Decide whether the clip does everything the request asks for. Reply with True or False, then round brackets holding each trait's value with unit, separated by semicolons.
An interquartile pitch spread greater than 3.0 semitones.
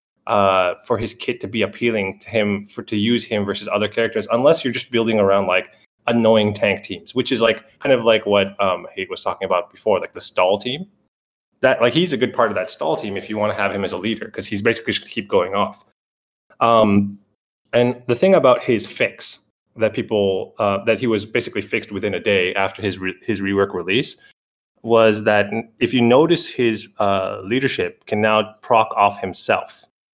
False (2.7 semitones)